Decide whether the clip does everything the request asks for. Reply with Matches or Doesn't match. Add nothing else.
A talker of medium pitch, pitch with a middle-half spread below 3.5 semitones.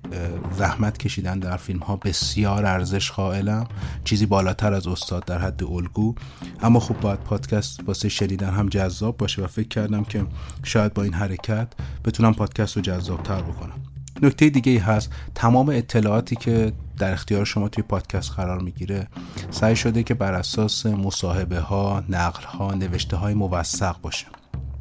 Doesn't match